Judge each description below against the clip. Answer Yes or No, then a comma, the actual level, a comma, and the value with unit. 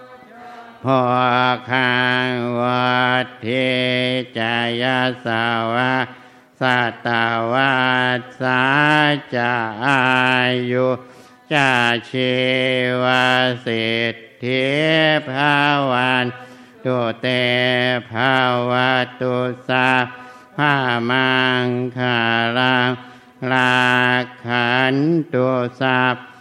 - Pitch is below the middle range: Yes, low, 125 Hz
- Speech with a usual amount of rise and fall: No, narrow, 0.6 semitones